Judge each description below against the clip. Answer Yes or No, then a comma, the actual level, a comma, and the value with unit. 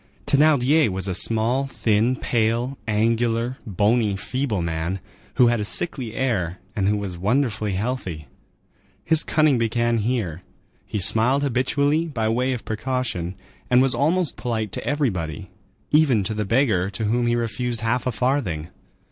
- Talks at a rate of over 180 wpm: No, average, 150 wpm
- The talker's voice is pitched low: Yes, low, 115 Hz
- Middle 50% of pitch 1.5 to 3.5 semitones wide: No, average, 4.0 semitones